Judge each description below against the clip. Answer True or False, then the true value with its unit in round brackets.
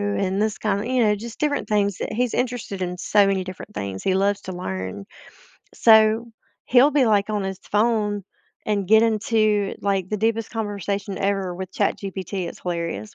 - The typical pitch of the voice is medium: False (205 Hz)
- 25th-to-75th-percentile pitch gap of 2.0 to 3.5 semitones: True (2.5 semitones)